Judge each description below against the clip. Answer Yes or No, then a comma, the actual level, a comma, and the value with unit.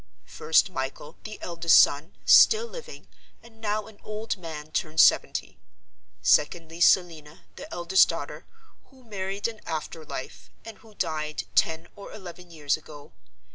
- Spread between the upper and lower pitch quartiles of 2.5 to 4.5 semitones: No, average, 5.1 semitones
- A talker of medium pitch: Yes, medium, 170 Hz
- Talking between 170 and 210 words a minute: No, average, 140 wpm